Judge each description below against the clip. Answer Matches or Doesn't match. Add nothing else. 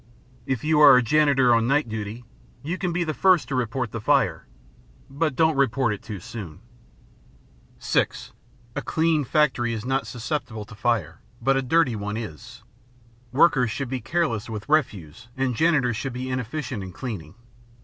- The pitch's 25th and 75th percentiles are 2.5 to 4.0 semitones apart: Doesn't match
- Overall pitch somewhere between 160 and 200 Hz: Doesn't match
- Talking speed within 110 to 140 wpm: Doesn't match